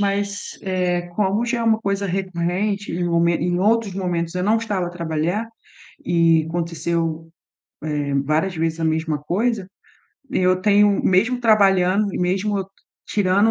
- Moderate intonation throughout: Yes, average, 3.2 semitones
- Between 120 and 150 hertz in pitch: No, medium, 185 Hz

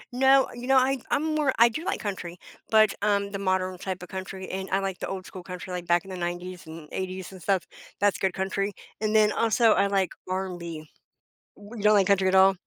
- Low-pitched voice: No, high, 190 Hz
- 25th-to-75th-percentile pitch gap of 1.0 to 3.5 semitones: Yes, narrow, 2.4 semitones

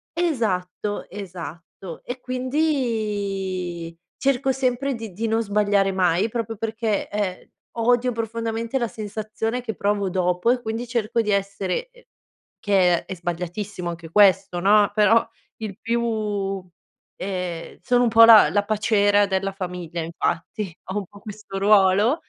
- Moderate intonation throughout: Yes, average, 3.4 semitones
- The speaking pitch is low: No, high, 210 Hz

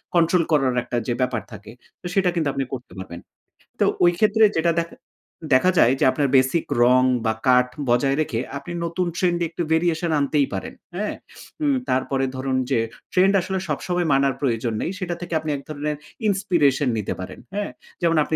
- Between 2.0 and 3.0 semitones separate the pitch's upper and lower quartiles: No, average, 5.2 semitones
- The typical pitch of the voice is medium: Yes, medium, 150 Hz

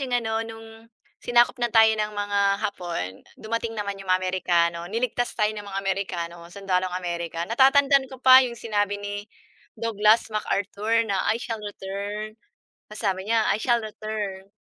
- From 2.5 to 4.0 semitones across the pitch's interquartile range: Yes, average, 2.9 semitones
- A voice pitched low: No, high, 210 Hz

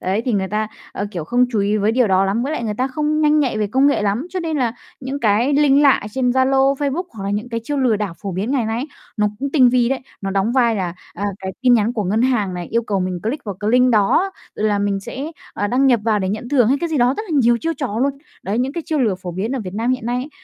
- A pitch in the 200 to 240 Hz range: Yes, high, 235 Hz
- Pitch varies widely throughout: No, average, 4.6 semitones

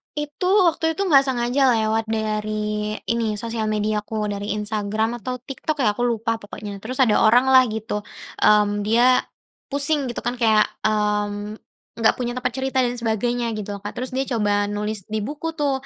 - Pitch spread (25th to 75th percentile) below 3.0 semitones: No, average, 3.3 semitones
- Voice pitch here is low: No, high, 225 Hz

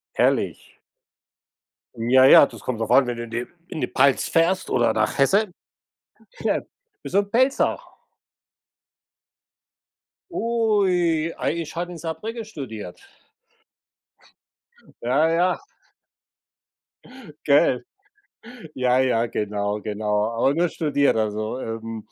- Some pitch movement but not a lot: No, wide, 7.3 semitones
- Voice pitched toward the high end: No, low, 135 Hz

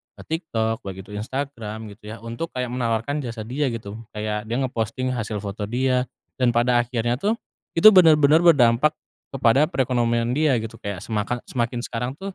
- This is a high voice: No, low, 120 Hz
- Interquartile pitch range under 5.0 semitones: Yes, average, 2.9 semitones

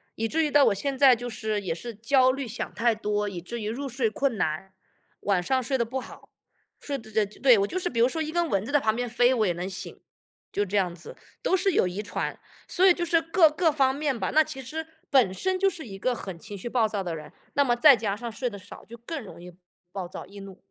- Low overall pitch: No, high, 235 Hz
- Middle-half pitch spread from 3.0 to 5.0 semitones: No, wide, 5.6 semitones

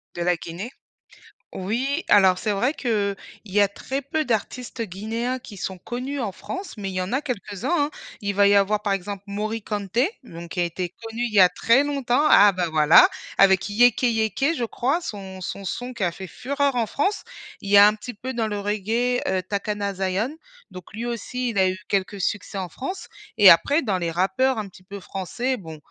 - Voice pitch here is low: No, high, 210 Hz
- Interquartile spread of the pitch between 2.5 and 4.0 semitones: No, average, 4.5 semitones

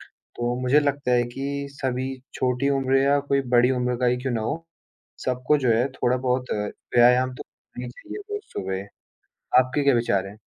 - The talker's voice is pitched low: Yes, low, 125 Hz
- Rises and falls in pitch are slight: Yes, narrow, 2.1 semitones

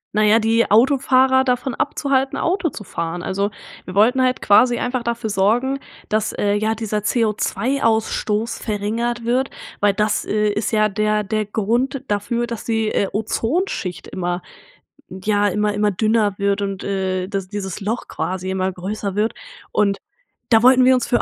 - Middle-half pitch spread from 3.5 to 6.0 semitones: No, average, 2.9 semitones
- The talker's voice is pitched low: No, high, 215 Hz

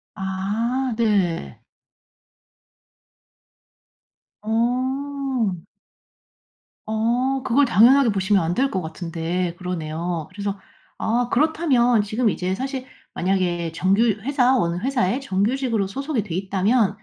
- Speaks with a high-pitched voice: Yes, high, 215 Hz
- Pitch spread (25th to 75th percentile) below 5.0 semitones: No, wide, 5.6 semitones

